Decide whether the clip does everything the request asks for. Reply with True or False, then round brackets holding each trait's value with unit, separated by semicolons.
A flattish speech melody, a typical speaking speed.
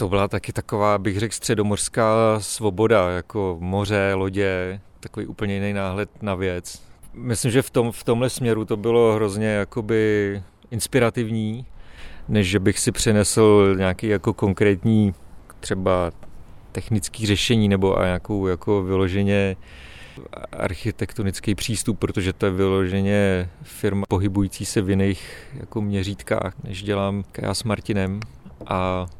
True (2.3 semitones; 130 wpm)